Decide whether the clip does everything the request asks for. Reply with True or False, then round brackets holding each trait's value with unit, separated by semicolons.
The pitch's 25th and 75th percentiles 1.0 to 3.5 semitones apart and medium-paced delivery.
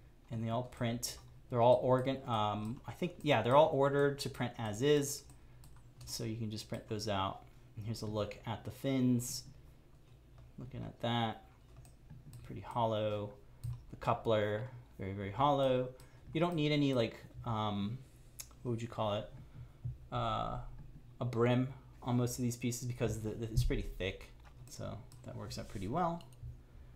True (2.5 semitones; 165 wpm)